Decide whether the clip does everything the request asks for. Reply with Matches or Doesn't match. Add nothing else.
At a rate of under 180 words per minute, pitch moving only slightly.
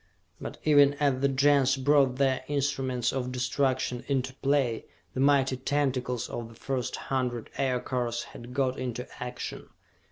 Matches